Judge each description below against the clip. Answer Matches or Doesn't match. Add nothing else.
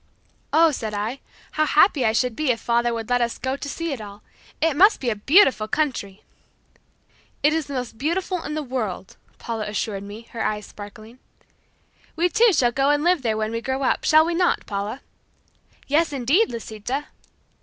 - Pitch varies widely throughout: Matches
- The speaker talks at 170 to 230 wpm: Matches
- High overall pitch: Matches